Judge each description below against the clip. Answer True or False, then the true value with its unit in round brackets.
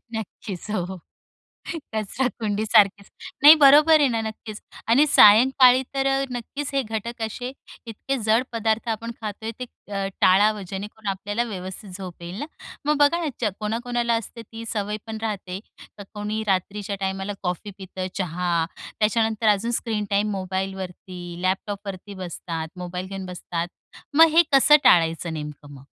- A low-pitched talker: False (210 Hz)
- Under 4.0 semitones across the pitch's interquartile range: True (3.5 semitones)